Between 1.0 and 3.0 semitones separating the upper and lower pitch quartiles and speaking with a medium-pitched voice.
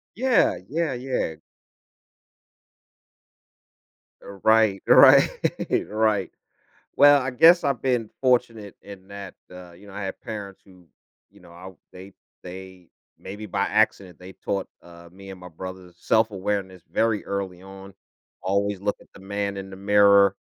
No: narrow, 2.5 semitones; low, 100 Hz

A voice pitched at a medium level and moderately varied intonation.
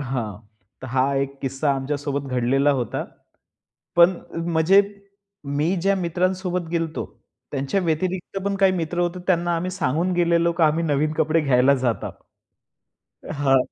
Yes: medium, 160 Hz; average, 4.2 semitones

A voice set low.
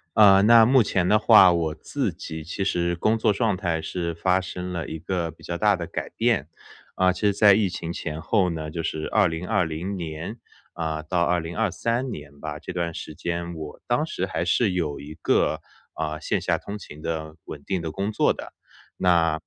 Yes: very low, 85 Hz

